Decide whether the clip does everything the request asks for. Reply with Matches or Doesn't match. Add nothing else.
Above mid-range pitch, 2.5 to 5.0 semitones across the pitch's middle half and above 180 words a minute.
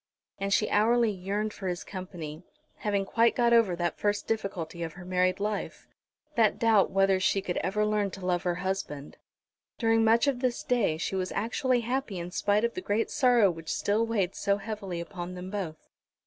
Matches